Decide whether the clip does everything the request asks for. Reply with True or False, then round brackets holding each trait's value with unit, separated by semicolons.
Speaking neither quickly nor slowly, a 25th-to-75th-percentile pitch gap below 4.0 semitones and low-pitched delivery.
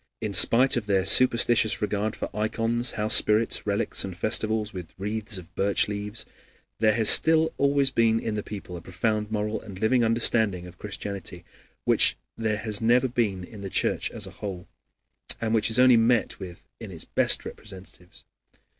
True (170 wpm; 2.6 semitones; 110 Hz)